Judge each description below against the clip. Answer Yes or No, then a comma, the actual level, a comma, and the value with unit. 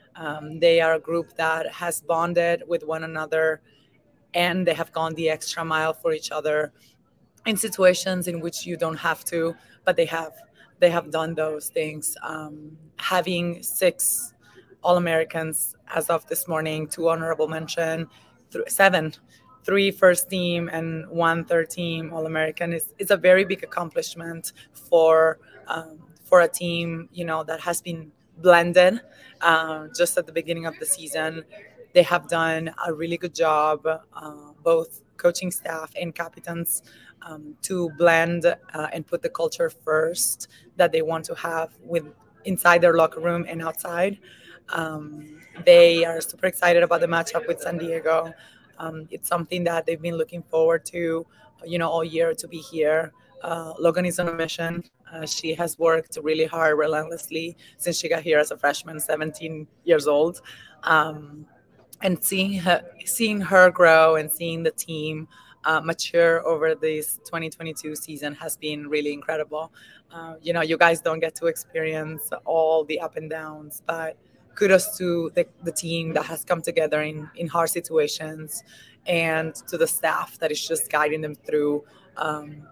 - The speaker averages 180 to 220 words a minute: No, average, 165 wpm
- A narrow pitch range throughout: Yes, narrow, 1.5 semitones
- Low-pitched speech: No, medium, 165 Hz